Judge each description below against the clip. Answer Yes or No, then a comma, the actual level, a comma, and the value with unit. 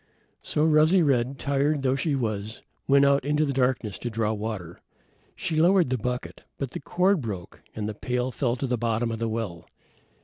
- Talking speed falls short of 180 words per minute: No, average, 195 wpm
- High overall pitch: No, low, 125 Hz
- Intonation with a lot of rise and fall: No, average, 4.1 semitones